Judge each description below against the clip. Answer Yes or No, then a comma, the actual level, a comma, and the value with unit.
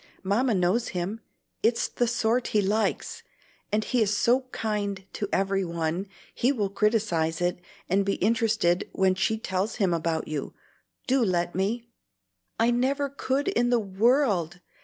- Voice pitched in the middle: No, high, 205 Hz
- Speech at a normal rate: Yes, average, 155 wpm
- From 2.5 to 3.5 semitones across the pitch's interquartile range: No, average, 4.0 semitones